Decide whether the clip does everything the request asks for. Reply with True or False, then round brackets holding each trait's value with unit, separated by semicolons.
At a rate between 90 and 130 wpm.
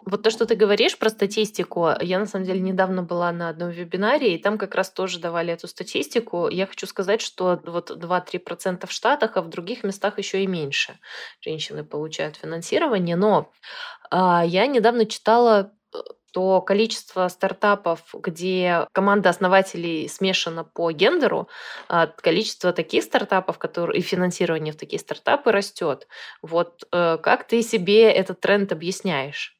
False (145 wpm)